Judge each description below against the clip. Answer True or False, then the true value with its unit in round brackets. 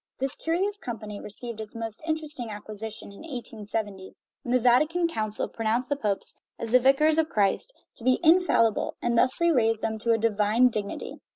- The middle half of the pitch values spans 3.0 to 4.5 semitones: False (4.9 semitones)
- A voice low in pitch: False (230 Hz)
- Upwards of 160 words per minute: True (180 wpm)